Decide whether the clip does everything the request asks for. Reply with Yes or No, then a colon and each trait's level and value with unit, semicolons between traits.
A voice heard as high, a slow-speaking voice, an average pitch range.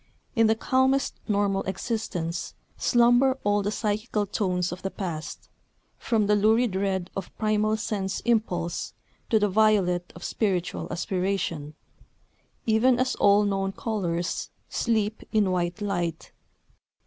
Yes: high, 205 Hz; slow, 125 wpm; average, 3.2 semitones